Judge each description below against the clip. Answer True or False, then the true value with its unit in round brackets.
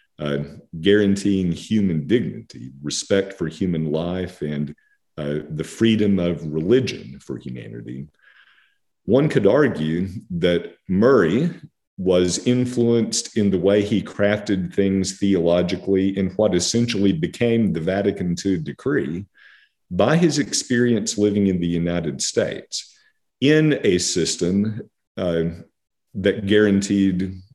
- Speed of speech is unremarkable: False (115 wpm)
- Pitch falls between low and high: False (95 Hz)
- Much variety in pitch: False (3.3 semitones)